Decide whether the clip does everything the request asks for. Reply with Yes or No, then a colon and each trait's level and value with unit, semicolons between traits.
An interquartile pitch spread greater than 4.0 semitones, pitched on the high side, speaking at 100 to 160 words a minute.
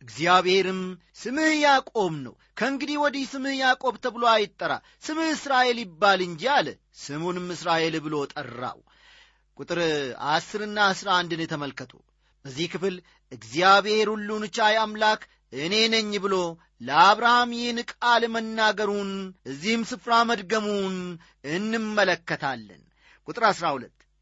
Yes: average, 5.3 semitones; high, 205 Hz; average, 105 wpm